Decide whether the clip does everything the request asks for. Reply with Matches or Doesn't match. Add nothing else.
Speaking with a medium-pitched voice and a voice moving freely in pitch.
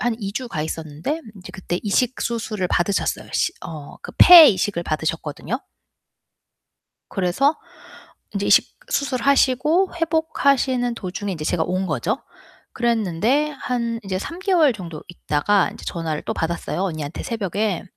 Doesn't match